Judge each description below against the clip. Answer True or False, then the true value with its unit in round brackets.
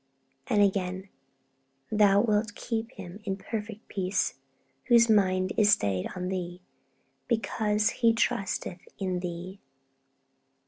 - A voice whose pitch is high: True (200 Hz)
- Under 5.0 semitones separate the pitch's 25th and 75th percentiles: True (2.8 semitones)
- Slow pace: True (110 wpm)